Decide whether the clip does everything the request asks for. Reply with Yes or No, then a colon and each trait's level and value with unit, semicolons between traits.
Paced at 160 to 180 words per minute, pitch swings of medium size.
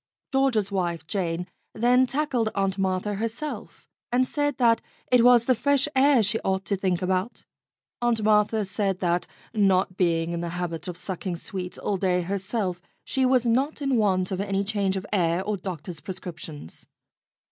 Yes: average, 170 wpm; average, 4.5 semitones